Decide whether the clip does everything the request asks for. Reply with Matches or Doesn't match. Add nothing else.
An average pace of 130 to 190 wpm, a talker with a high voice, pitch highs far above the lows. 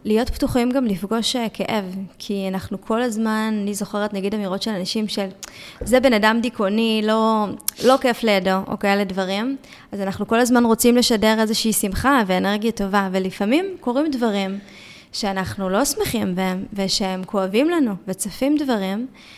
Doesn't match